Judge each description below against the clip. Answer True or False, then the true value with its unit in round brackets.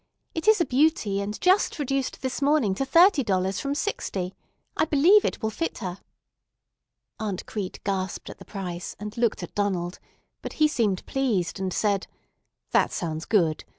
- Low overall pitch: False (210 Hz)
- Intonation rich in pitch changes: True (7.0 semitones)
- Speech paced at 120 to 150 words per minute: False (170 wpm)